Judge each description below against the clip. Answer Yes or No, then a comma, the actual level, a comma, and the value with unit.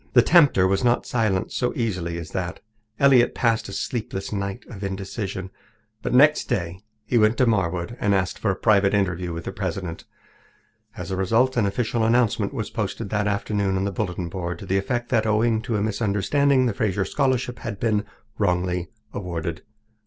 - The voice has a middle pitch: No, low, 100 Hz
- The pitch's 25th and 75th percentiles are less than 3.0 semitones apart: No, average, 3.8 semitones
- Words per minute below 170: No, average, 180 wpm